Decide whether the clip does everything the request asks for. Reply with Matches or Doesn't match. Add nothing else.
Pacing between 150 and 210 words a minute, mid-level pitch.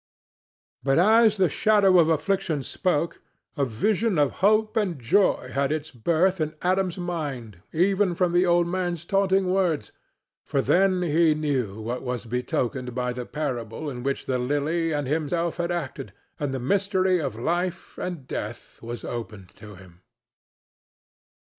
Matches